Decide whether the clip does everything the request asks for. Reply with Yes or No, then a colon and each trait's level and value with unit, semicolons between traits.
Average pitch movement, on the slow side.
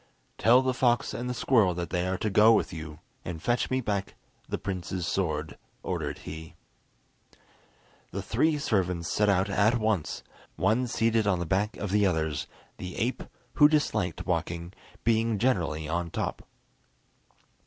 No: average, 4.9 semitones; average, 155 wpm